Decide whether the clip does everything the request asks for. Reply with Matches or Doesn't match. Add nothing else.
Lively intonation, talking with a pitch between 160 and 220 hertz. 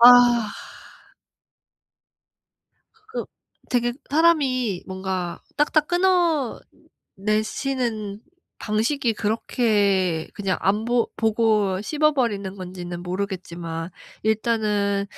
Doesn't match